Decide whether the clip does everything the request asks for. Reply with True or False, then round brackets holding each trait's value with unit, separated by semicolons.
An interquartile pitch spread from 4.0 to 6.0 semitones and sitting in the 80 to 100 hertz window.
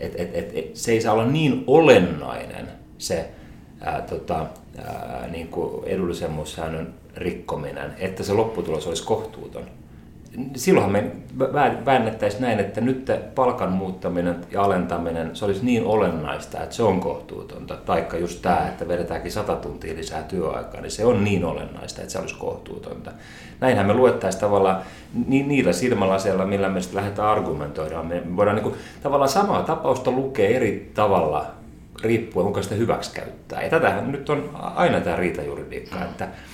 True (4.3 semitones; 95 Hz)